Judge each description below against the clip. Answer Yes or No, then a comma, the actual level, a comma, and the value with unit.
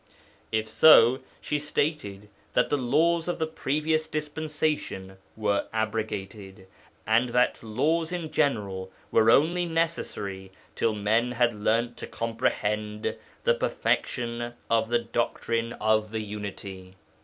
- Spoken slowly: Yes, slow, 120 wpm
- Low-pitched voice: Yes, low, 115 Hz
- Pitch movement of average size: No, wide, 6.0 semitones